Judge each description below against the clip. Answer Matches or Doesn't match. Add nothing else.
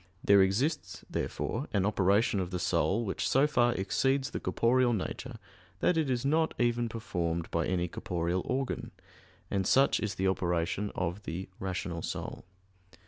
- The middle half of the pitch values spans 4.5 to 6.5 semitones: Matches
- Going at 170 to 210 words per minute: Doesn't match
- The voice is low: Matches